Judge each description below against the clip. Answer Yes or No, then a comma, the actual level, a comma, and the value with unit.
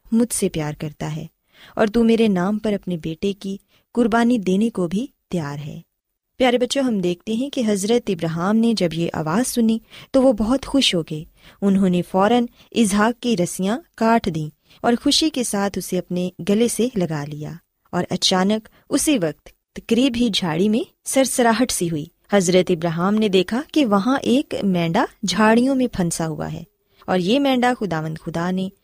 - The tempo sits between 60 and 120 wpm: Yes, average, 115 wpm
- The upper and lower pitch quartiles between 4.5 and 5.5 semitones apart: Yes, average, 5.0 semitones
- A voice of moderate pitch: No, high, 205 Hz